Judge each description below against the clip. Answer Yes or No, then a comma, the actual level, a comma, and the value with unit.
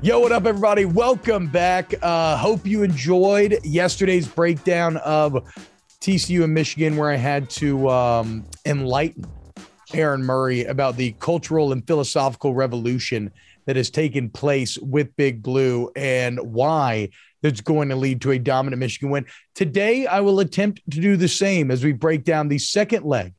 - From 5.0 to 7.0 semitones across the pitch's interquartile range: Yes, average, 5.3 semitones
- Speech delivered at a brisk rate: No, average, 160 wpm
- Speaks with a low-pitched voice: No, medium, 150 Hz